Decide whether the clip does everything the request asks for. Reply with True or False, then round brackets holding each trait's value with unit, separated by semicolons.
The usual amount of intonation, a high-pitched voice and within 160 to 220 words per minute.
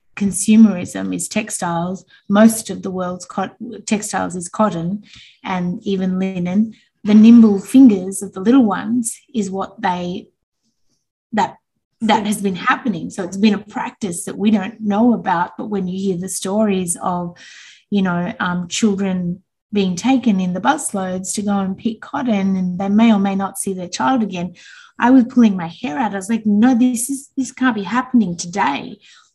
True (3.4 semitones; 200 Hz; 180 wpm)